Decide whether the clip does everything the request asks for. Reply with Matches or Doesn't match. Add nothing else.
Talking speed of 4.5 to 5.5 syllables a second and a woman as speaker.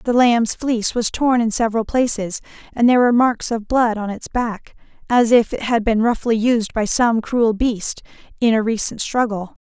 Matches